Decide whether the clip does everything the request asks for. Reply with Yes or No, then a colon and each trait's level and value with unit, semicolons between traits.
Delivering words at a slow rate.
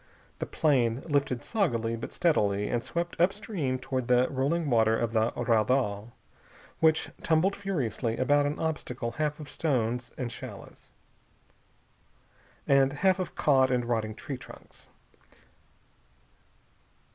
Yes: slow, 125 wpm